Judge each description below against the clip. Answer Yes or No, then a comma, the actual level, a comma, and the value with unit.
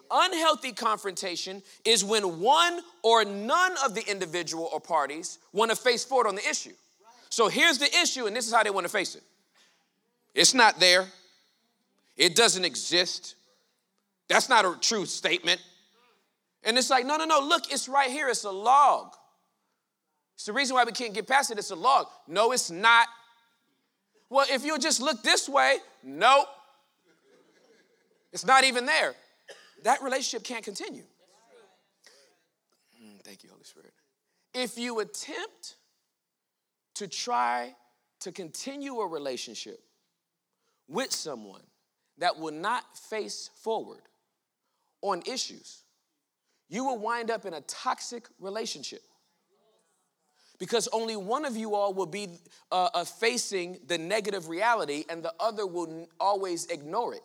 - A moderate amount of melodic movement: No, wide, 6.0 semitones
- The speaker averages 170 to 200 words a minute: No, average, 145 wpm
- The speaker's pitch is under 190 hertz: No, high, 225 Hz